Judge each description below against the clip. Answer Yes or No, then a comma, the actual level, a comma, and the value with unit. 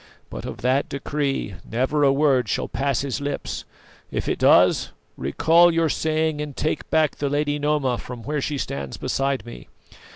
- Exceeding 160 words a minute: Yes, average, 170 wpm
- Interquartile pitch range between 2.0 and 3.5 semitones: Yes, narrow, 2.5 semitones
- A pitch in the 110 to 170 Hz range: Yes, medium, 140 Hz